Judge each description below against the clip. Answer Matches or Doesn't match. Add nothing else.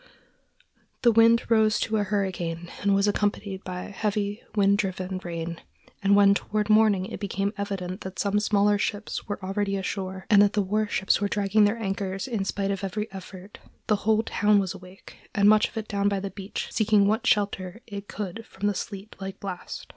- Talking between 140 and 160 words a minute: Doesn't match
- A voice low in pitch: Doesn't match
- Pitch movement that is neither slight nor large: Doesn't match